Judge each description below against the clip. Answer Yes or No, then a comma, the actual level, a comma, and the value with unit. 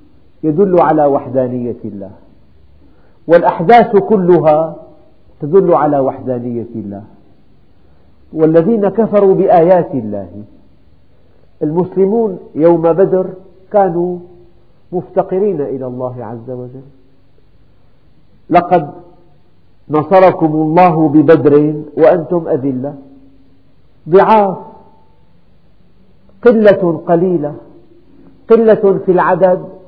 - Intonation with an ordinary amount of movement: No, wide, 7.8 semitones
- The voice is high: No, medium, 155 Hz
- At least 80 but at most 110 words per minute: No, average, 70 wpm